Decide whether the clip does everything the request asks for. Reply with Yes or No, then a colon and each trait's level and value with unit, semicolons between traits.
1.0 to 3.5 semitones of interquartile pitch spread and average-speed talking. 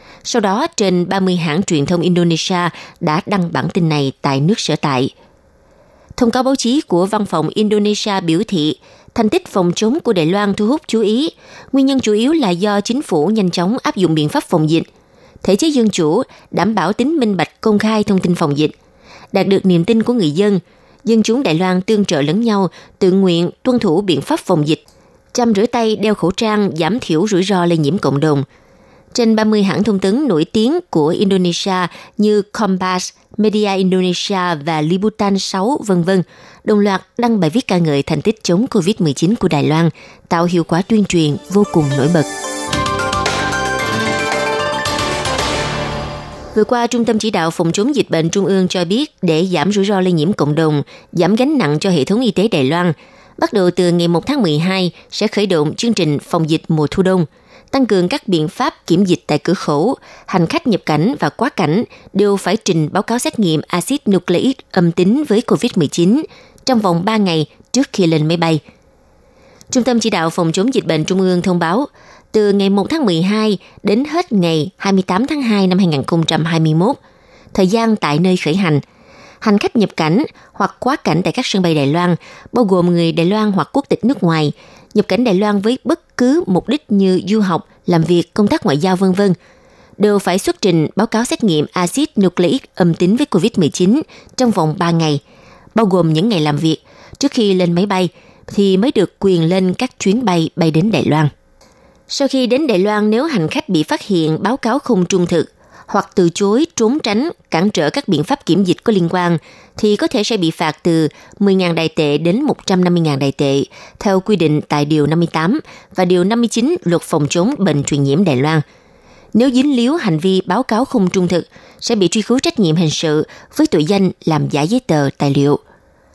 No: average, 4.7 semitones; average, 210 wpm